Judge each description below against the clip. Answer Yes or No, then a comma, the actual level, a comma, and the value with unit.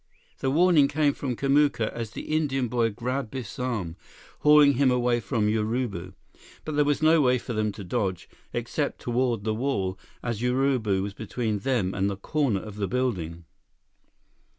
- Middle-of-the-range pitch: No, low, 120 Hz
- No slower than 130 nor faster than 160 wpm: No, average, 170 wpm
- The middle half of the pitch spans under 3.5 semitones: No, average, 4.7 semitones